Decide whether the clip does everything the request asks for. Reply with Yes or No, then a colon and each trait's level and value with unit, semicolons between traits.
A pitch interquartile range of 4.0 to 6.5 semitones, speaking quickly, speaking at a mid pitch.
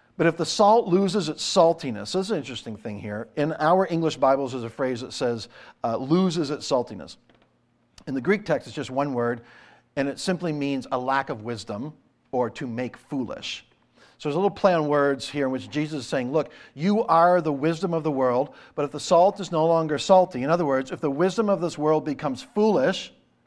Yes: average, 4.8 semitones; fast, 220 wpm; medium, 150 Hz